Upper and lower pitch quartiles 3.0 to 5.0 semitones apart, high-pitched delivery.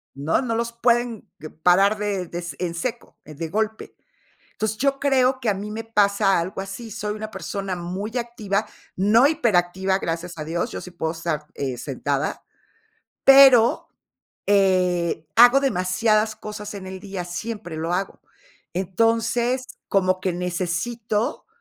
Yes: average, 4.4 semitones; high, 200 Hz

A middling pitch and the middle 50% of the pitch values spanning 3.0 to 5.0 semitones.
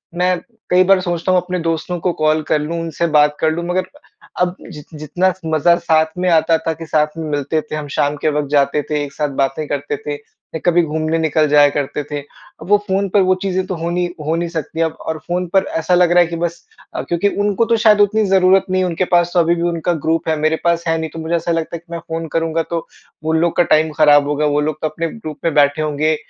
No: medium, 165 Hz; narrow, 2.5 semitones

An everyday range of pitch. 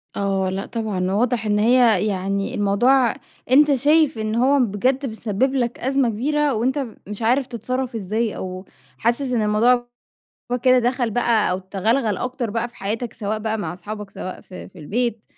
Yes: average, 3.5 semitones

